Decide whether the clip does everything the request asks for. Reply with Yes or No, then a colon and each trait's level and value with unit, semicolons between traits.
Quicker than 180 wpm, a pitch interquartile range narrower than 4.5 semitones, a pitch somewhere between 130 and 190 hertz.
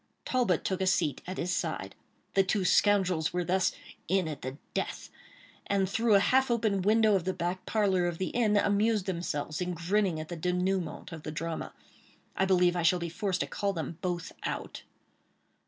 Yes: average, 190 wpm; average, 2.7 semitones; medium, 185 Hz